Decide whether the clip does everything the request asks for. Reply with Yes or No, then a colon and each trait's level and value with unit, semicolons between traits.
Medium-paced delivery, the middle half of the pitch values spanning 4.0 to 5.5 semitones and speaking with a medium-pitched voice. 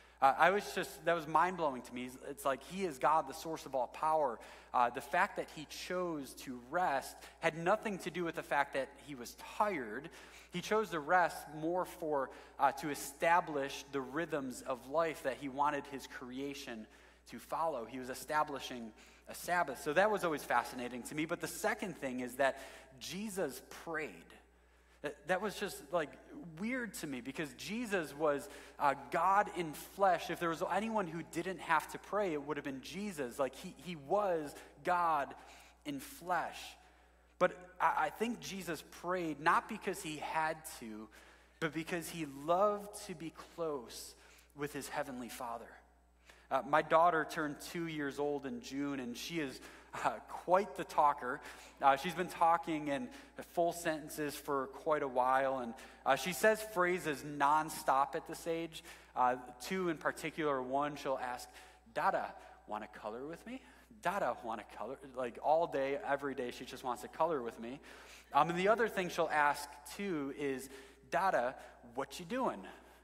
Yes: average, 175 wpm; average, 4.4 semitones; medium, 155 Hz